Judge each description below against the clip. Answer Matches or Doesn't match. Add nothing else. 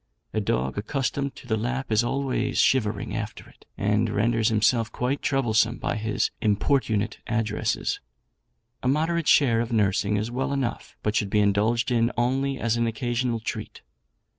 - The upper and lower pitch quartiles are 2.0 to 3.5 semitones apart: Matches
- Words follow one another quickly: Doesn't match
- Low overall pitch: Matches